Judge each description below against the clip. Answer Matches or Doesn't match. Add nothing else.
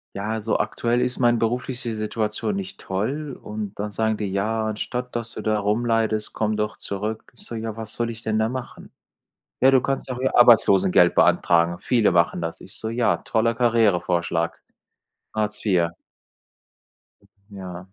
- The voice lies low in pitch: Matches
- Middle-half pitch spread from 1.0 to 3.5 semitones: Matches